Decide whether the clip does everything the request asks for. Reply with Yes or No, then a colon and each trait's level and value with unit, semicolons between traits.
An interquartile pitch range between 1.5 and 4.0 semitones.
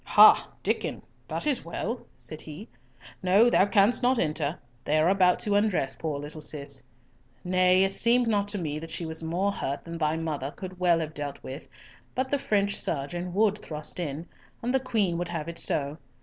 No: average, 4.8 semitones